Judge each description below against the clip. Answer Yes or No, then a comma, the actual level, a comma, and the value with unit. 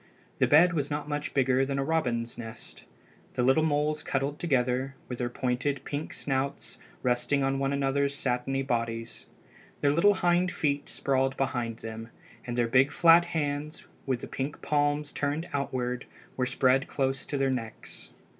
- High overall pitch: No, low, 135 Hz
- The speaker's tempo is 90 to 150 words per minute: No, average, 165 wpm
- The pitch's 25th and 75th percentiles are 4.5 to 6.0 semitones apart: No, narrow, 2.6 semitones